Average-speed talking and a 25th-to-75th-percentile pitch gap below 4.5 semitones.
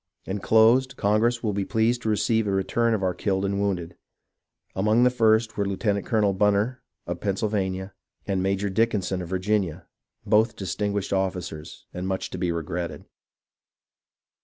Yes: average, 155 wpm; average, 2.7 semitones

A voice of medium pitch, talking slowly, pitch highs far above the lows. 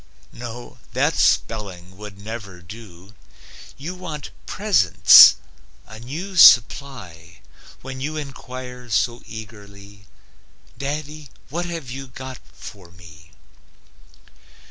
No: low, 120 Hz; slow, 100 wpm; wide, 5.7 semitones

